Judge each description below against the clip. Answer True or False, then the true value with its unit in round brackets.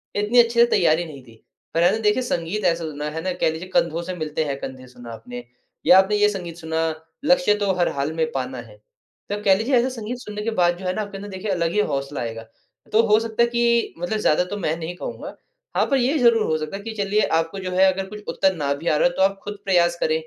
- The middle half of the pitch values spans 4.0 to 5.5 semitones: True (5.0 semitones)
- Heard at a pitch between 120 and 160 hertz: False (185 Hz)